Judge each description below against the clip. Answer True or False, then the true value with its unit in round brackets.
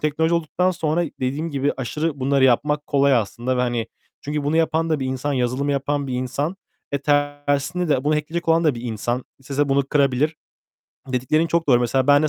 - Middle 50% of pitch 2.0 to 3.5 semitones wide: True (2.9 semitones)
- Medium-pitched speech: True (145 Hz)